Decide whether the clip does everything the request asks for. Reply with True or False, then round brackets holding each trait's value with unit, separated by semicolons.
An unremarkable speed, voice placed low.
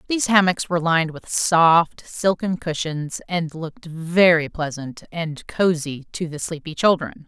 False (150 wpm; 165 Hz)